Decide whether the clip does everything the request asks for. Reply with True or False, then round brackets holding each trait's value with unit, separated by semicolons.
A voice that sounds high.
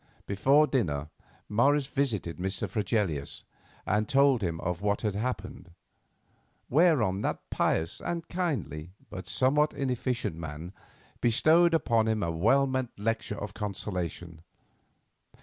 False (105 Hz)